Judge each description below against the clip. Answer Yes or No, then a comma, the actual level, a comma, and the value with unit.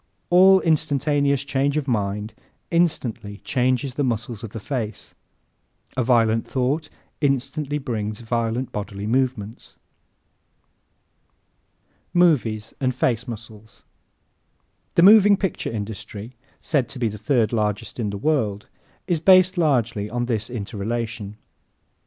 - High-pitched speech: No, low, 120 Hz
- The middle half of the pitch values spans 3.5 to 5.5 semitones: Yes, average, 4.8 semitones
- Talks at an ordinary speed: No, slow, 120 wpm